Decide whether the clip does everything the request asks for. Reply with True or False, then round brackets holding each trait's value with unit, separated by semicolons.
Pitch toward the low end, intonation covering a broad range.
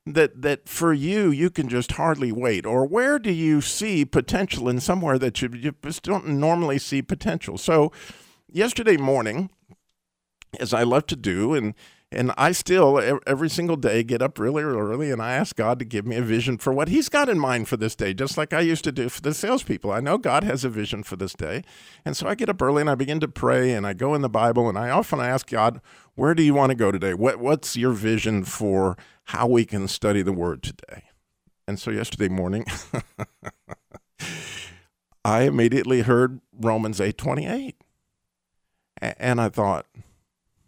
True (130 Hz; 5.8 semitones)